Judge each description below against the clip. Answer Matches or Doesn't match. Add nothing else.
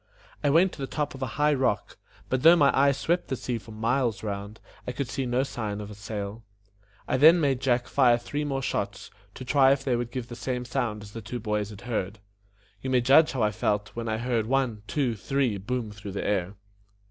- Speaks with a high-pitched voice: Doesn't match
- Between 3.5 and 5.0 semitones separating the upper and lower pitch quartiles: Matches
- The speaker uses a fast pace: Matches